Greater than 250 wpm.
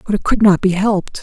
Yes: fast, 295 wpm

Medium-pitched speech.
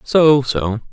No: low, 125 Hz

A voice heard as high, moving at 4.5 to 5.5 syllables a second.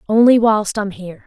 Yes: high, 210 Hz; 5.4 syllables/s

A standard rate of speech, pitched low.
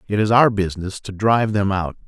No: fast, 230 wpm; low, 100 Hz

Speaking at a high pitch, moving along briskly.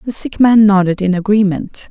No: high, 205 Hz; average, 190 wpm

